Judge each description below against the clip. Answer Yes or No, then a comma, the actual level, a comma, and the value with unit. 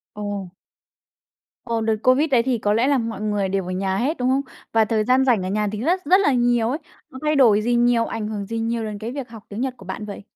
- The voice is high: Yes, high, 230 Hz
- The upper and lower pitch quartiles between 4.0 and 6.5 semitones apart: No, average, 3.4 semitones